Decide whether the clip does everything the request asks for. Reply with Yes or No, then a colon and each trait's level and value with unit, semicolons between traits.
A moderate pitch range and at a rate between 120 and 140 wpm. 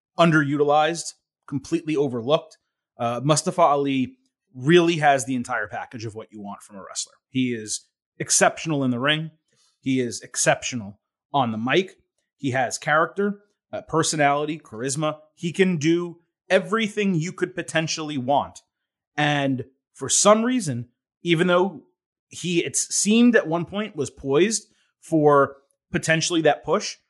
Yes: average, 4.4 semitones; slow, 135 wpm